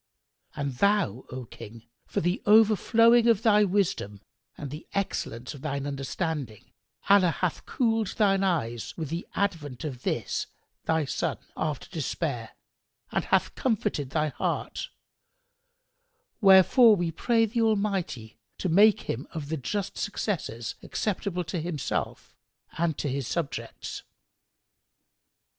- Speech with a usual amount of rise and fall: No, wide, 6.6 semitones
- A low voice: No, medium, 170 Hz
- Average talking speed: No, slow, 125 wpm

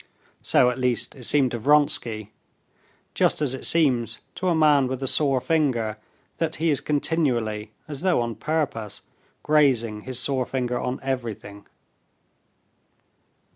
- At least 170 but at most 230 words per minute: No, average, 140 wpm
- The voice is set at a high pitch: No, low, 130 Hz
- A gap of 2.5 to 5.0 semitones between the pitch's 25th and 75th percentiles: Yes, average, 4.0 semitones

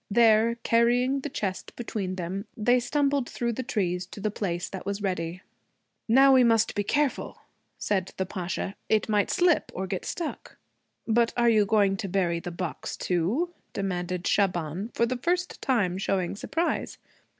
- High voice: Yes, high, 205 Hz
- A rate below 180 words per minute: Yes, average, 165 wpm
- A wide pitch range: No, average, 4.6 semitones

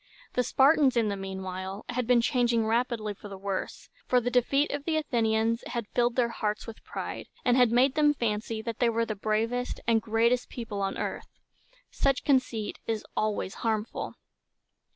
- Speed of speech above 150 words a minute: Yes, average, 175 wpm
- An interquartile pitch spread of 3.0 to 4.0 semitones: No, narrow, 2.6 semitones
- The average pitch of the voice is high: Yes, high, 230 Hz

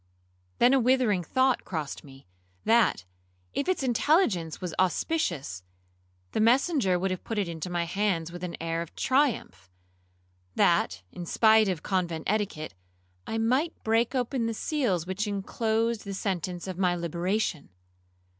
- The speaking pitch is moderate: No, high, 195 Hz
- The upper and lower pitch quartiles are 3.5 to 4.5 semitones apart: No, average, 5.3 semitones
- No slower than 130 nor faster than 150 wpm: Yes, average, 145 wpm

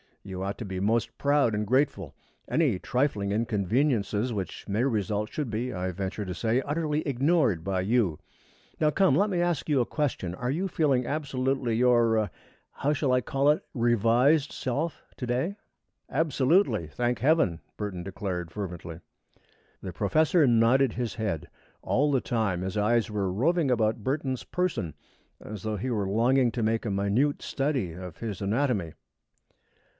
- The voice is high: No, low, 115 Hz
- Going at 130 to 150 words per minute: No, average, 160 wpm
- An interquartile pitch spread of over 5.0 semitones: Yes, wide, 5.5 semitones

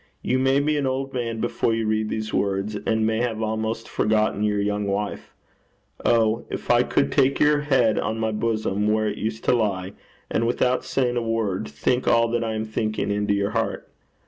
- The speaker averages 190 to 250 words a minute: Yes, average, 200 wpm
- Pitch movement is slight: Yes, narrow, 2.1 semitones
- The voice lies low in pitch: Yes, low, 110 Hz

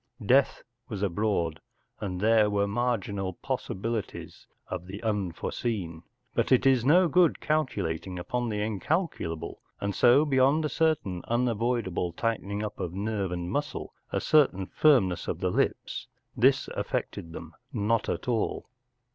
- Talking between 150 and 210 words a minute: No, average, 140 wpm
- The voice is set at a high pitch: No, low, 105 Hz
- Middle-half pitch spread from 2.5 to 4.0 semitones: No, average, 5.0 semitones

